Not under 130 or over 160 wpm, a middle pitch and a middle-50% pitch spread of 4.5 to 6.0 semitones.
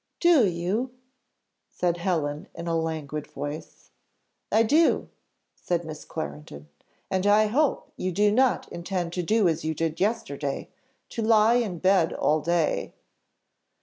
Yes: average, 140 wpm; medium, 175 Hz; average, 5.2 semitones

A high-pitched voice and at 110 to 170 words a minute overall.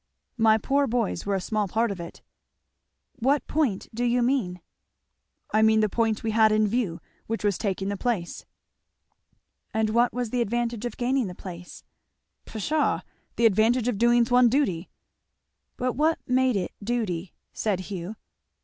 Yes: high, 225 Hz; average, 160 wpm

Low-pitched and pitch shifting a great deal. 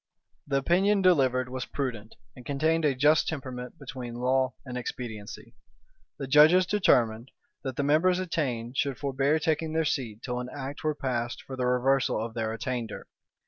No: low, 130 Hz; average, 3.5 semitones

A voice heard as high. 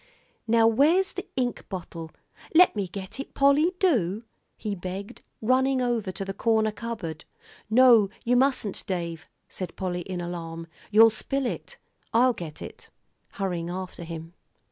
Yes: high, 210 Hz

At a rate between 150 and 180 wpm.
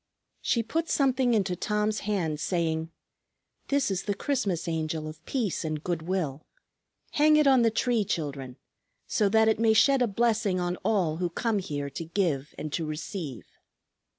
Yes: average, 170 wpm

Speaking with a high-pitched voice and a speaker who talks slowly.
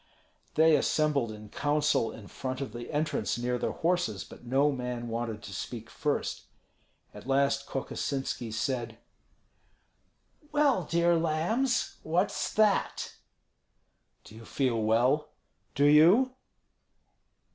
No: medium, 140 Hz; slow, 115 wpm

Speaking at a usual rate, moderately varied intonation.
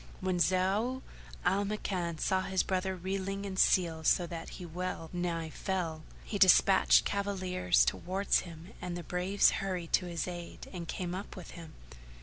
No: average, 160 wpm; narrow, 1.8 semitones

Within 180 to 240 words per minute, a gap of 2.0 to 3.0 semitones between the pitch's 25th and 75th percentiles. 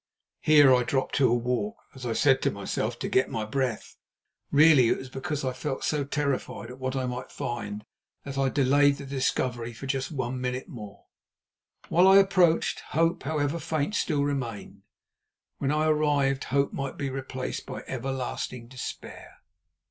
No: average, 165 wpm; narrow, 2.5 semitones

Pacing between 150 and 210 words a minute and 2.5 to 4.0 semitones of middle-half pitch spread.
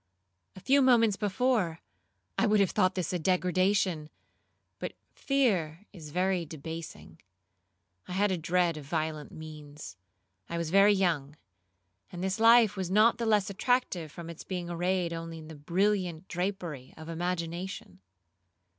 No: average, 140 wpm; average, 3.7 semitones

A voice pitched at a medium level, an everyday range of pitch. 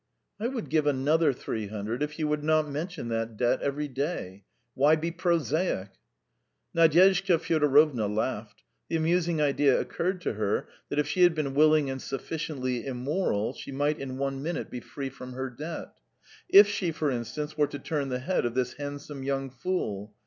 Yes: medium, 145 Hz; average, 3.9 semitones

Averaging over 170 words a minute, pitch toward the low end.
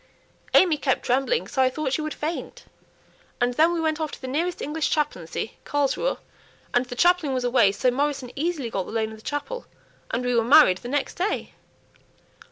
No: average, 195 wpm; very high, 275 Hz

